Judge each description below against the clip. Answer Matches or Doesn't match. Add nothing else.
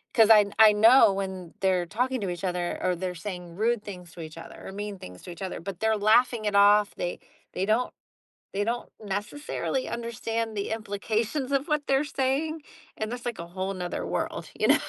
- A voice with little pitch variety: Doesn't match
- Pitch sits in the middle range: Doesn't match